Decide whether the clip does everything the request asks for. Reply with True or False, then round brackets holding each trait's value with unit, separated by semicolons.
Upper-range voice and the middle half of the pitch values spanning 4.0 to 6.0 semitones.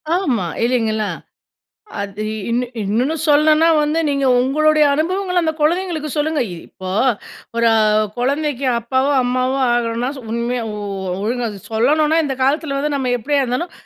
True (270 Hz; 4.3 semitones)